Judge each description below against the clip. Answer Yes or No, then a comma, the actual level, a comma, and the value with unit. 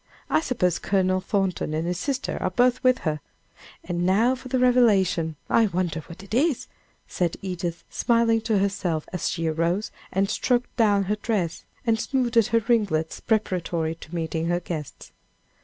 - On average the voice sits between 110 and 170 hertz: No, high, 195 Hz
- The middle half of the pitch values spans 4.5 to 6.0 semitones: Yes, average, 5.2 semitones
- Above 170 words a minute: No, average, 165 wpm